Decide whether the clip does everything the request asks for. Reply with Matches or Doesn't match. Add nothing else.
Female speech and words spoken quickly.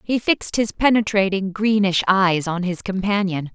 Doesn't match